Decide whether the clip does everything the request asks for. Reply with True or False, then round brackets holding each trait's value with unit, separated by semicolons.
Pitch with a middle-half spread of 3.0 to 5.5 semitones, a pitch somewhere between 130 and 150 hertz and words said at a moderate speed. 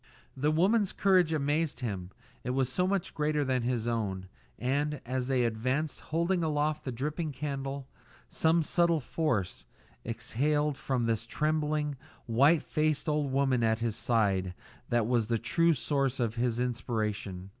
True (4.6 semitones; 135 Hz; 150 wpm)